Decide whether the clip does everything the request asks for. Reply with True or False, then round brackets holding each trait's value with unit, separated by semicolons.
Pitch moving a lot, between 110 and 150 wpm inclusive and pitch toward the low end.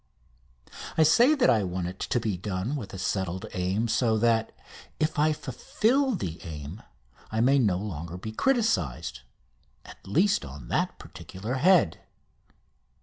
True (8.5 semitones; 145 wpm; 110 Hz)